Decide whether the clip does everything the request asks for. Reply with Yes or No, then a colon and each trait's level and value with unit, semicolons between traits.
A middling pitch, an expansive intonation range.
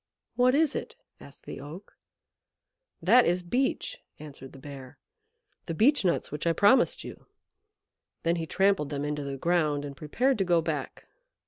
Yes: medium, 170 Hz; wide, 6.0 semitones